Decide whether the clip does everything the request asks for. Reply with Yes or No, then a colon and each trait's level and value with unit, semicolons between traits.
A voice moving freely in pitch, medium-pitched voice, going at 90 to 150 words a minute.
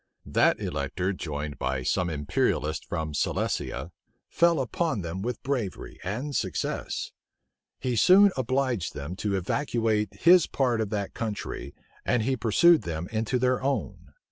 No: wide, 7.3 semitones; low, 110 Hz; average, 140 wpm